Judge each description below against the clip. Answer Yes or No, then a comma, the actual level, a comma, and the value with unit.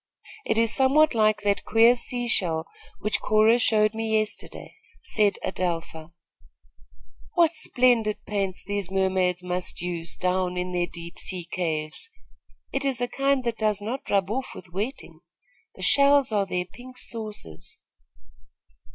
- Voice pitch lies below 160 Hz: No, high, 210 Hz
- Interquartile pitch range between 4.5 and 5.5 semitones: Yes, average, 4.9 semitones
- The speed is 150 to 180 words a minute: No, average, 140 wpm